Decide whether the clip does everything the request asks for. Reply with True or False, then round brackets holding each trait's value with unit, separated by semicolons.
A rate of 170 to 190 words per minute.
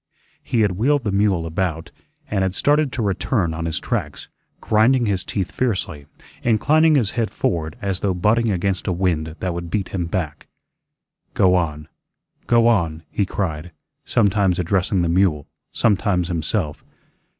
False (155 wpm)